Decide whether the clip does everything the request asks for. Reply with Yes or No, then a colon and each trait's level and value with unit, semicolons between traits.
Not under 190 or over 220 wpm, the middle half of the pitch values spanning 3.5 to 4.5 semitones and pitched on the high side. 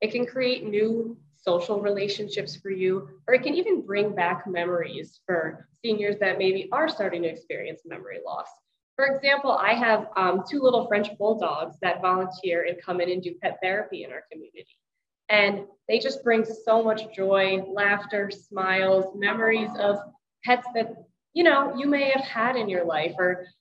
No: average, 175 wpm; average, 4.2 semitones; high, 205 Hz